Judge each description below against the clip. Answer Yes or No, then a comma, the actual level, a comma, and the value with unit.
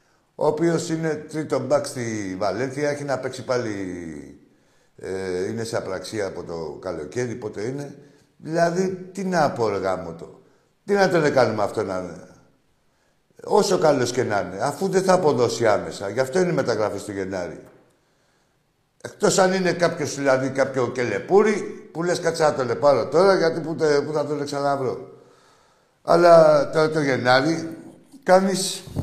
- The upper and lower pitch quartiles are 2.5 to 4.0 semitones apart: No, wide, 5.6 semitones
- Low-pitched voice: No, medium, 145 Hz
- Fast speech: No, average, 150 wpm